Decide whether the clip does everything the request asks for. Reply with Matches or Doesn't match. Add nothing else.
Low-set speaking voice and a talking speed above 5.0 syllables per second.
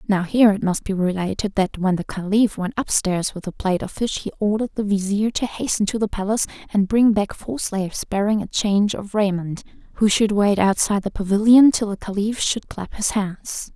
Doesn't match